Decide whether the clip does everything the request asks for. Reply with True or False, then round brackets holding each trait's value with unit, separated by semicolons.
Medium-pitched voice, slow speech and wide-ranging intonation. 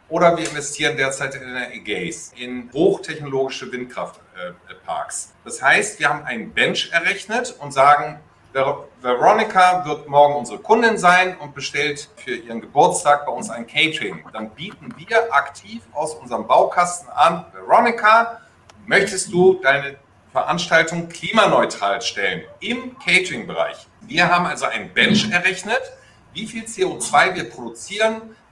False (160 Hz; 135 wpm; 6.9 semitones)